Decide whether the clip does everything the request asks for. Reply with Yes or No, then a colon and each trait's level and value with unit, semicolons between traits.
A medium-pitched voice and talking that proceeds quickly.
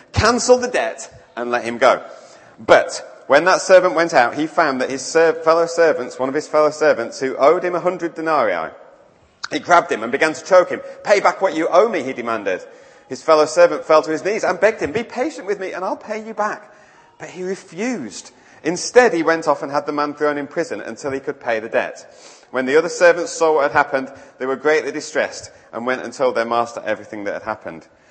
Yes: medium, 165 Hz; fast, 230 wpm